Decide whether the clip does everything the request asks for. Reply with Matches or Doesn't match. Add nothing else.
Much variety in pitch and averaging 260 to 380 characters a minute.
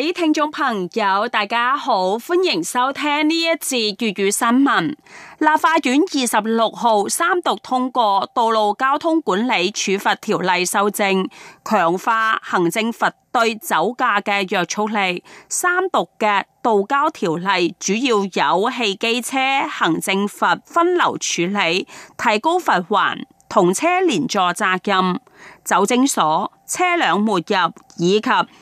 Doesn't match